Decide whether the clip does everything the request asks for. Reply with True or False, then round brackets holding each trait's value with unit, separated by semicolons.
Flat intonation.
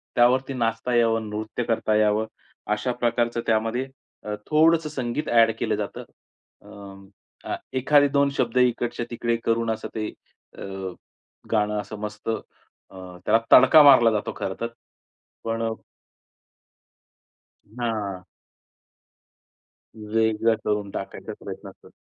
True (2.2 semitones)